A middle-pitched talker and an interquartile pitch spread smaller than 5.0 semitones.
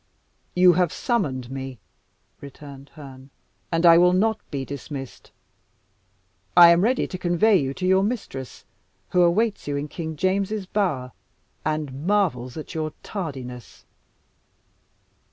No: medium, 165 Hz; wide, 5.5 semitones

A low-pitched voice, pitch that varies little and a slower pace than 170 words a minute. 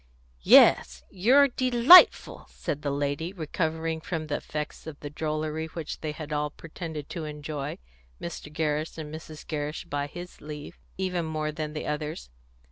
No: medium, 155 Hz; narrow, 1.7 semitones; average, 155 wpm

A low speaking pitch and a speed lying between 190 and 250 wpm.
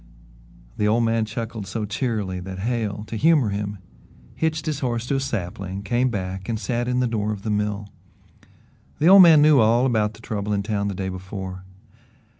Yes: low, 110 Hz; average, 195 wpm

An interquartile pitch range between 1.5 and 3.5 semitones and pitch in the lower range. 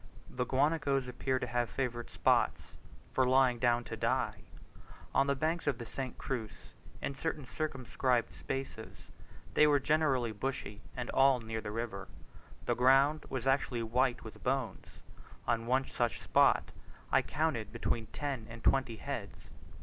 Yes: narrow, 2.5 semitones; low, 130 Hz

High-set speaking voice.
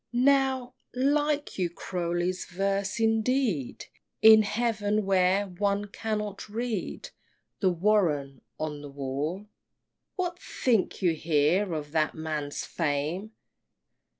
Yes: high, 195 Hz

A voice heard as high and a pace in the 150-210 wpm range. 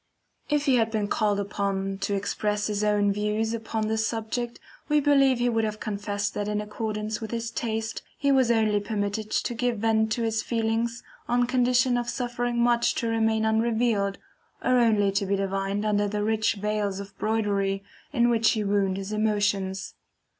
Yes: high, 220 Hz; average, 180 wpm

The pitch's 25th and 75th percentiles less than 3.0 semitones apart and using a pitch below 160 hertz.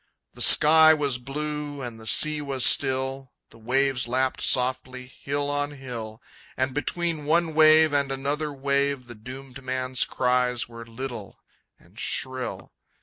Yes: narrow, 2.4 semitones; low, 135 Hz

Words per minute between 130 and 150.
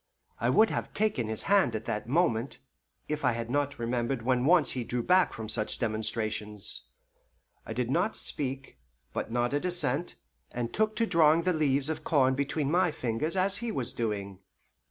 No: average, 175 wpm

